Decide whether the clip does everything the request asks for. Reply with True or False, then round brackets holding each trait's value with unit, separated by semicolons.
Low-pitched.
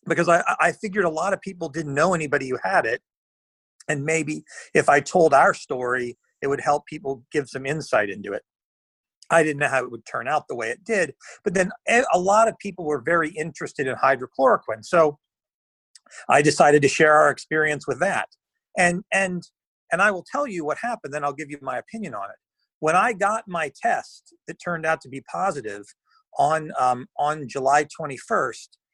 False (160 Hz)